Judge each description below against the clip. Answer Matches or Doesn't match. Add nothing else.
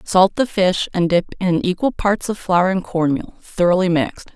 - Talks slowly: Doesn't match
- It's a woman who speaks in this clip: Matches